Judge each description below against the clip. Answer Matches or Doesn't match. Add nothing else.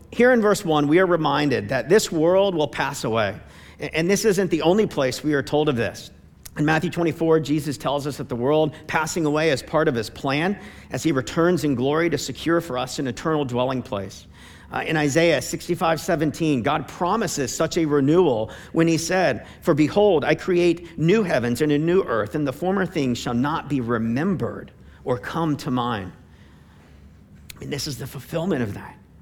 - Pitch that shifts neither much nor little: Matches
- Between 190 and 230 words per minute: Matches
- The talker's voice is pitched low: Doesn't match